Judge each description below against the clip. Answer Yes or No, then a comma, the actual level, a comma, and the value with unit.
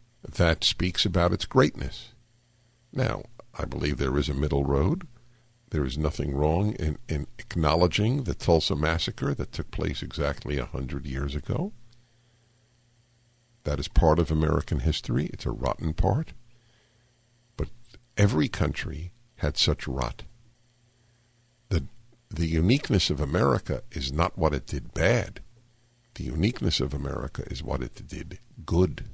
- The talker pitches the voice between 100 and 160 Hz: No, very low, 90 Hz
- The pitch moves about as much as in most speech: No, wide, 7.5 semitones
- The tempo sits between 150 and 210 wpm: No, average, 140 wpm